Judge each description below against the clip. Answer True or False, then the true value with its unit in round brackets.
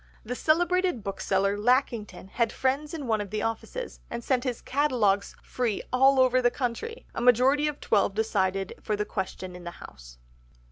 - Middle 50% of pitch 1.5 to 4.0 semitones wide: False (4.8 semitones)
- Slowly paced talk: False (175 wpm)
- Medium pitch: False (235 Hz)